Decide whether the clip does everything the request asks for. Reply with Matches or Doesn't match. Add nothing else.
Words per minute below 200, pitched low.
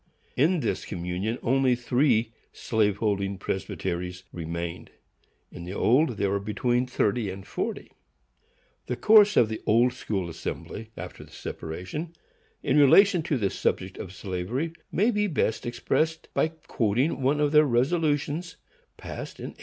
Matches